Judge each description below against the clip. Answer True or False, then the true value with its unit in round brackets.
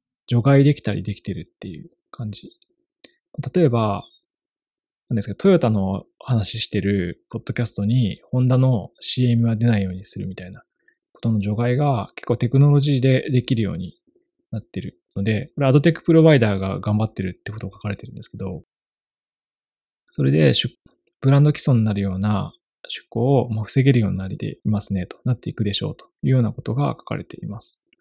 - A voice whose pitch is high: False (120 Hz)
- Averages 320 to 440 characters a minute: True (375 characters per minute)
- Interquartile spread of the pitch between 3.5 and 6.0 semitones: True (5.4 semitones)